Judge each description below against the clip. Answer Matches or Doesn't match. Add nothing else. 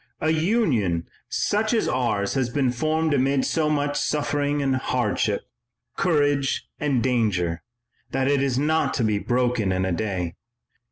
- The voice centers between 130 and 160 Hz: Matches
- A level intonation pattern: Doesn't match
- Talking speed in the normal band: Matches